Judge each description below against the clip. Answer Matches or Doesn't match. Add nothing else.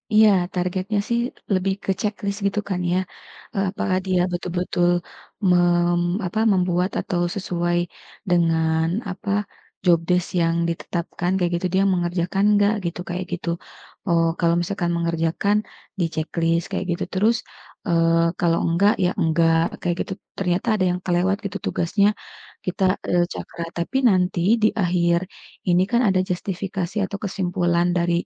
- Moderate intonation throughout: Doesn't match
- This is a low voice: Doesn't match